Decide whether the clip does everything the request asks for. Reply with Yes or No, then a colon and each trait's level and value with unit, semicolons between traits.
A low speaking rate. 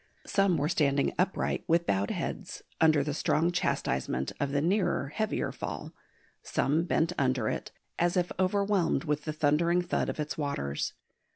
No: average, 160 wpm